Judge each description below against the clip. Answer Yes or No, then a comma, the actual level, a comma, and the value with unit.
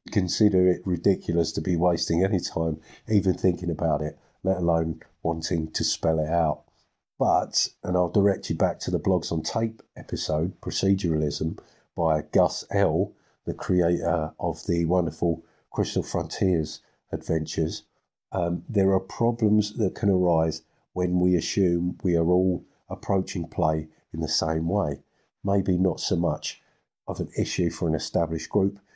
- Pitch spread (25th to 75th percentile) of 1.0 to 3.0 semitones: Yes, narrow, 2.6 semitones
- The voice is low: Yes, very low, 85 Hz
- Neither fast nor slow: Yes, average, 150 wpm